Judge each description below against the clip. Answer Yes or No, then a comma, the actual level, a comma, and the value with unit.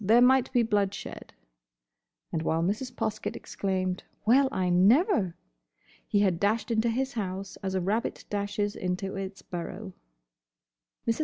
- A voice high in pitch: Yes, high, 205 Hz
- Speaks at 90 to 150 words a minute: Yes, average, 140 wpm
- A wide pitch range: No, average, 3.6 semitones